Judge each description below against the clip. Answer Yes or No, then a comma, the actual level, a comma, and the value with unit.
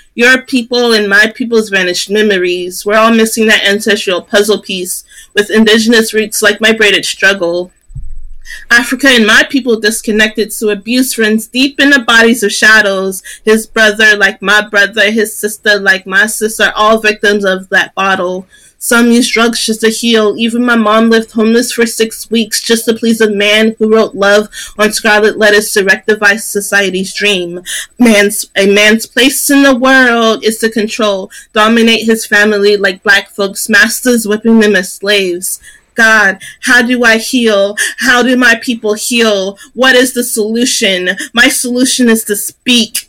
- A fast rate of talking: No, average, 170 wpm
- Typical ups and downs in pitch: No, narrow, 2.2 semitones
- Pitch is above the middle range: Yes, high, 215 Hz